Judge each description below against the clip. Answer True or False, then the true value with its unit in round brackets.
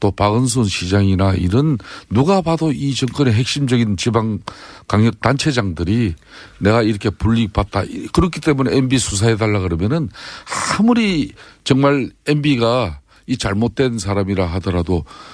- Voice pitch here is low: True (115 Hz)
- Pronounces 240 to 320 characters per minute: True (300 characters per minute)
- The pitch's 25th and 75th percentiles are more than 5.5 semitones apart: False (5.2 semitones)